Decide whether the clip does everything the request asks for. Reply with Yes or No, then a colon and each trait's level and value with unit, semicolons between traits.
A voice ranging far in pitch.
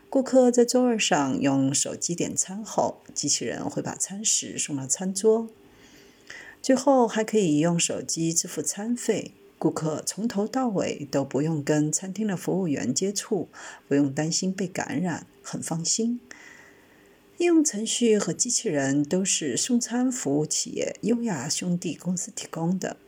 Yes: wide, 6.6 semitones